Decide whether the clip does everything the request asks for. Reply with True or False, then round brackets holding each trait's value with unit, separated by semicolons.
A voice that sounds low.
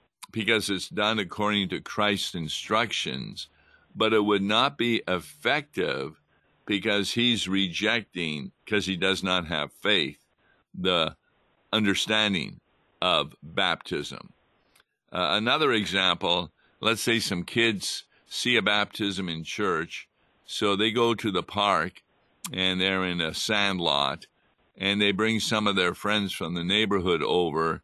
True (100 Hz)